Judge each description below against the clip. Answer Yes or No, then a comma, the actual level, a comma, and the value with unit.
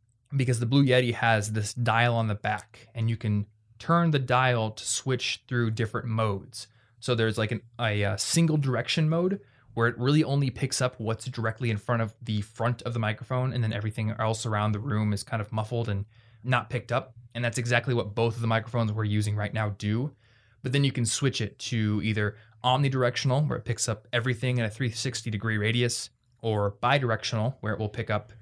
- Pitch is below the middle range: Yes, low, 115 Hz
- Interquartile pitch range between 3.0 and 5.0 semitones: No, narrow, 2.4 semitones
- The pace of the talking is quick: Yes, fast, 210 wpm